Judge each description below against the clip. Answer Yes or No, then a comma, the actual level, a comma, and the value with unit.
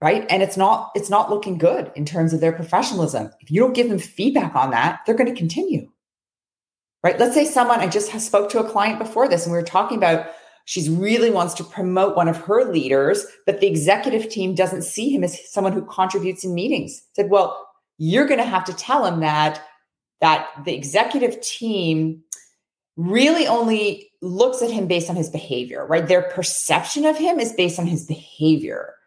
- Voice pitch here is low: No, medium, 185 Hz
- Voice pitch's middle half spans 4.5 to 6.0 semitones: Yes, average, 5.2 semitones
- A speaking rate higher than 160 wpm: Yes, average, 200 wpm